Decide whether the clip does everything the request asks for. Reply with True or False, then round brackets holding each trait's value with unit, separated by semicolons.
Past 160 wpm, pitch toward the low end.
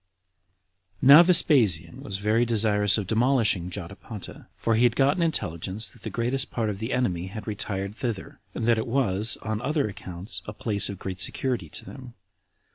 True (180 wpm; 110 Hz)